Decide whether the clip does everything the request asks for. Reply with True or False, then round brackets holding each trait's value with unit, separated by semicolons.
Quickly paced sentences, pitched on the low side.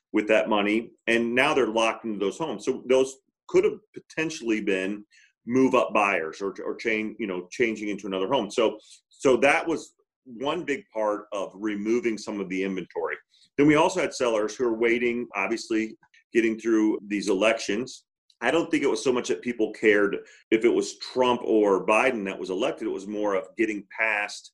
False (195 wpm; 110 Hz)